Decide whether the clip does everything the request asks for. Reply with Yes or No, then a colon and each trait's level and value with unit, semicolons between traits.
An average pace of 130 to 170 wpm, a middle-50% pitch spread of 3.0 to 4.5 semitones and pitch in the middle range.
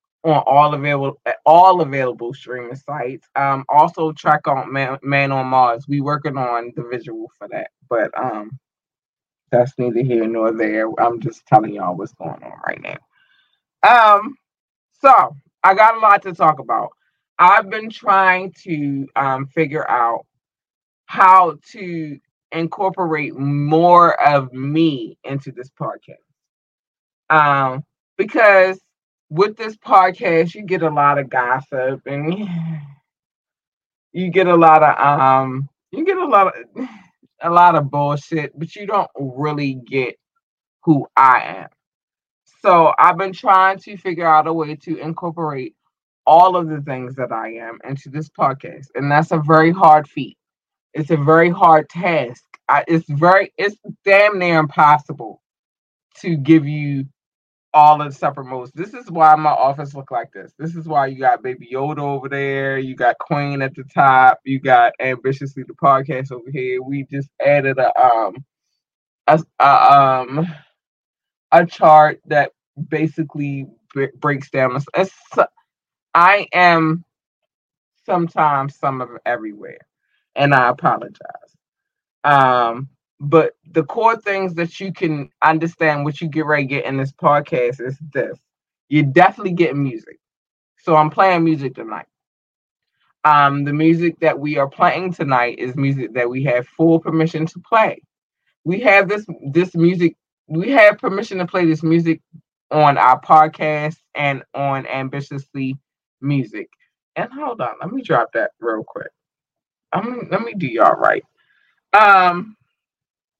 Yes: average, 150 wpm; average, 4.1 semitones; medium, 155 Hz